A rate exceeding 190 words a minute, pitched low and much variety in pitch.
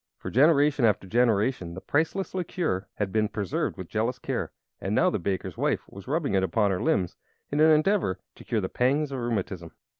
Yes: average, 200 wpm; low, 115 Hz; wide, 7.1 semitones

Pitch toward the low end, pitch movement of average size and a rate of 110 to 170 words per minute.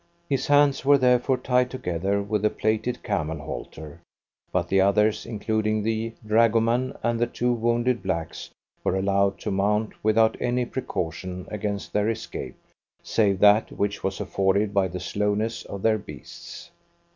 Yes: low, 105 Hz; average, 3.1 semitones; average, 150 wpm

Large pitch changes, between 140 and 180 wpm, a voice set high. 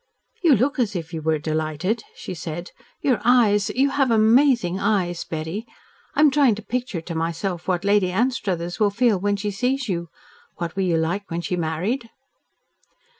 Yes: wide, 5.8 semitones; average, 175 wpm; high, 200 Hz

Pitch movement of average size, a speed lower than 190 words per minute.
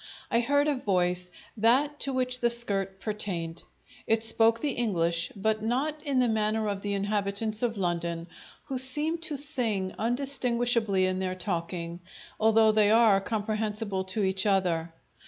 Yes: average, 4.1 semitones; average, 155 wpm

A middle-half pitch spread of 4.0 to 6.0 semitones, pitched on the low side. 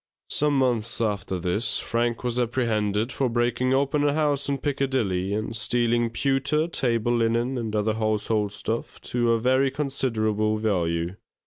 No: average, 3.5 semitones; low, 115 Hz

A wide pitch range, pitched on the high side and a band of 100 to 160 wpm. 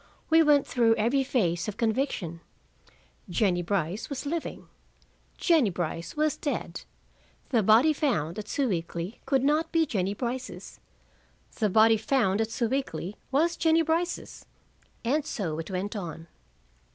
Yes: wide, 7.3 semitones; high, 225 Hz; slow, 135 wpm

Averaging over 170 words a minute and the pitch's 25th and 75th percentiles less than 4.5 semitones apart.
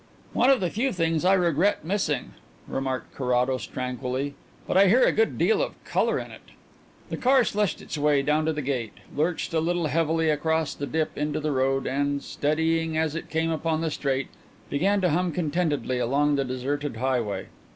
Yes: average, 190 wpm; average, 3.5 semitones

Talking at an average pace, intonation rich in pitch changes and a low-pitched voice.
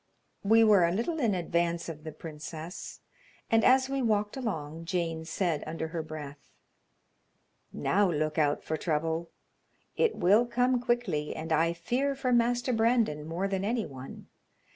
No: average, 155 wpm; wide, 6.5 semitones; medium, 175 Hz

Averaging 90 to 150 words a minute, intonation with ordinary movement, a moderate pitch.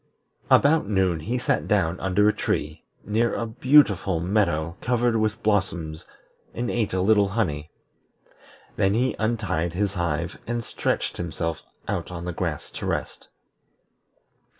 No: average, 140 wpm; average, 4.6 semitones; very low, 95 Hz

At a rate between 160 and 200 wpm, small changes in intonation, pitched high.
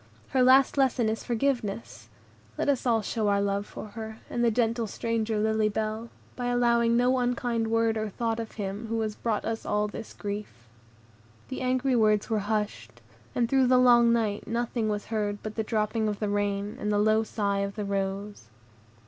Yes: average, 190 wpm; narrow, 2.3 semitones; high, 220 Hz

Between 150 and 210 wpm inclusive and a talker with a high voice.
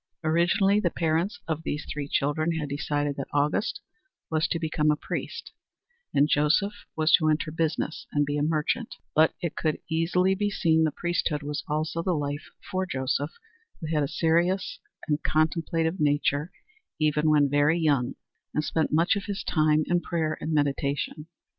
No: average, 170 wpm; medium, 155 Hz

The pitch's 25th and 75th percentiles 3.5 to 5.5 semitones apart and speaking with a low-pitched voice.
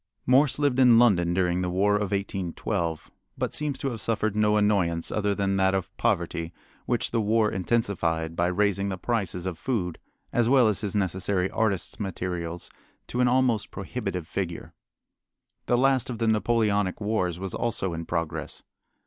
Yes: average, 4.1 semitones; low, 100 Hz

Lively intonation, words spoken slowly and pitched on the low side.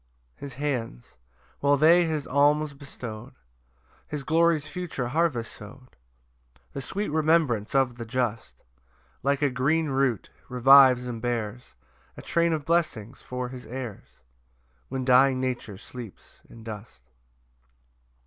No: average, 3.7 semitones; slow, 130 wpm; low, 130 Hz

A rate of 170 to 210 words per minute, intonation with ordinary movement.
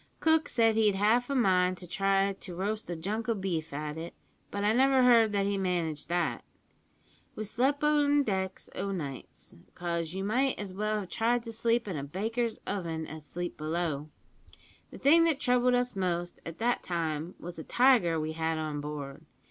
No: average, 190 wpm; wide, 5.7 semitones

